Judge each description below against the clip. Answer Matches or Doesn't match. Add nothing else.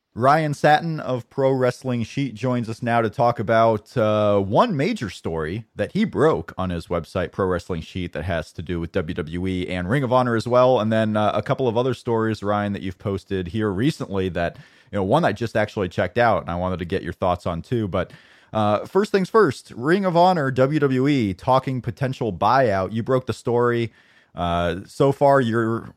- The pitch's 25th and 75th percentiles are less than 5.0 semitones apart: Doesn't match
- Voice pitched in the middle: Doesn't match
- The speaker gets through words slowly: Doesn't match